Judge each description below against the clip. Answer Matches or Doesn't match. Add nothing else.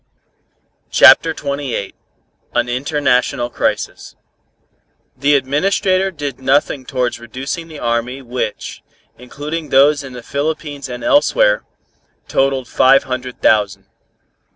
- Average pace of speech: Doesn't match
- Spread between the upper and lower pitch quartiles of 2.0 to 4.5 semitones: Matches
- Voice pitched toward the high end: Doesn't match